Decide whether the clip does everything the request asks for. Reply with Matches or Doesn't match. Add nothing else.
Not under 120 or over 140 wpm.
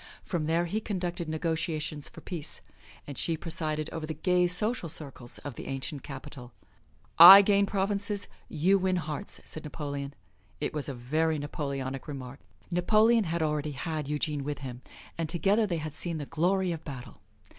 Doesn't match